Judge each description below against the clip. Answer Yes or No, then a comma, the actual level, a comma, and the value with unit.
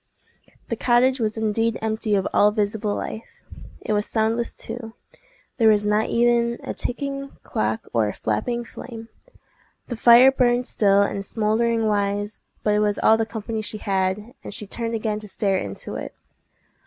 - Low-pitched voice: No, high, 220 Hz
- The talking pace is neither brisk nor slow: Yes, average, 165 wpm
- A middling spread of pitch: No, narrow, 2.2 semitones